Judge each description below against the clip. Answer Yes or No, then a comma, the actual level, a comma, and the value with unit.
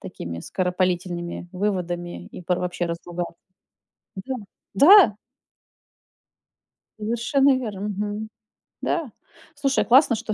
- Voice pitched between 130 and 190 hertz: No, high, 200 Hz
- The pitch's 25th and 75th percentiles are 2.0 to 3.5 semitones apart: No, average, 5.1 semitones